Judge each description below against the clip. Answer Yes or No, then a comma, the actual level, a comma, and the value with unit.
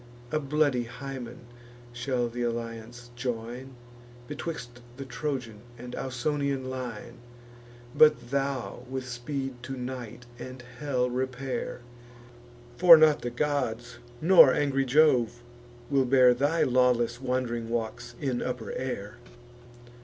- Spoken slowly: Yes, slow, 115 wpm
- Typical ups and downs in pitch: No, narrow, 2.1 semitones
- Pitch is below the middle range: Yes, low, 125 Hz